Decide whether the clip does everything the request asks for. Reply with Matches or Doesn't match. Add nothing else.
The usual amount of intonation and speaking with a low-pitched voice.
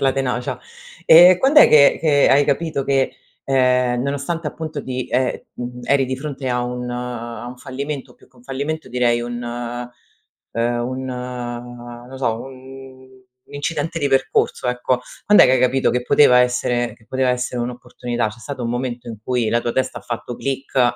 Doesn't match